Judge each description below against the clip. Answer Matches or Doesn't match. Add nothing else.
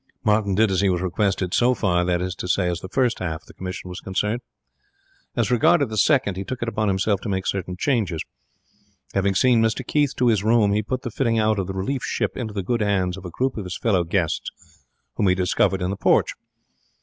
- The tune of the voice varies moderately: Matches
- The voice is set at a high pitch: Doesn't match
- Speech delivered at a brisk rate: Matches